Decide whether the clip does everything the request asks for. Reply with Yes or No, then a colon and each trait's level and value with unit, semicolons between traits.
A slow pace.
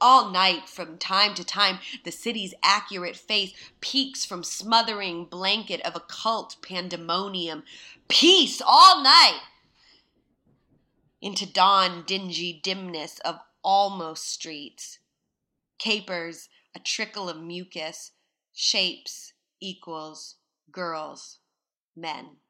Yes: slow, 95 wpm